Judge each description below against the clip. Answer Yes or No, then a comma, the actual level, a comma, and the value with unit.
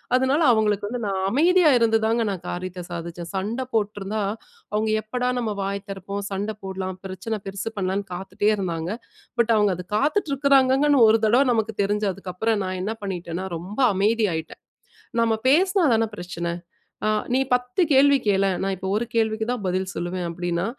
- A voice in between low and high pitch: No, high, 205 Hz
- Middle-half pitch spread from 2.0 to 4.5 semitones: Yes, average, 3.5 semitones